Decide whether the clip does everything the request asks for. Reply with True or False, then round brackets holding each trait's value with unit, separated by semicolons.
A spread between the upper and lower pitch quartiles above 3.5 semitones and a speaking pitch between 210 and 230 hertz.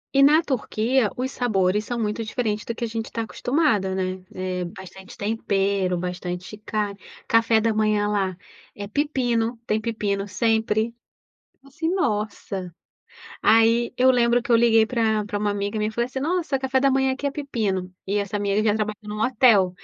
False (3.2 semitones; 220 Hz)